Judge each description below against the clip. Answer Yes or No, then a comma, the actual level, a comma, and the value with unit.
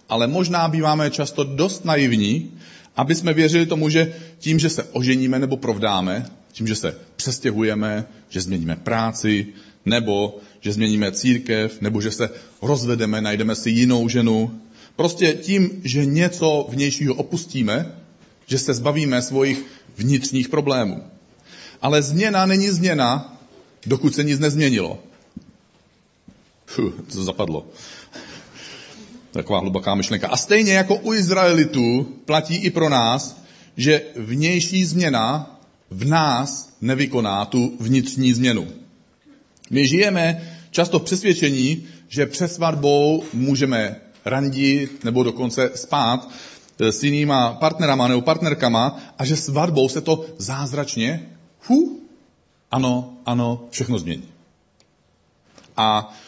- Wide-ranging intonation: Yes, wide, 5.7 semitones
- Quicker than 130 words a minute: No, slow, 115 wpm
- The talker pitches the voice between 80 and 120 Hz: No, low, 135 Hz